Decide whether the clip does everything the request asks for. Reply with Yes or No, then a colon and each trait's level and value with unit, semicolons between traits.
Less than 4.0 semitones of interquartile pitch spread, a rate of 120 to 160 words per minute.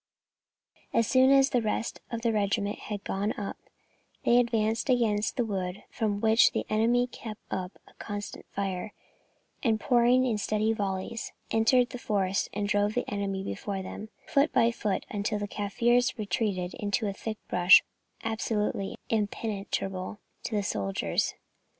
Yes: narrow, 2.4 semitones; average, 150 wpm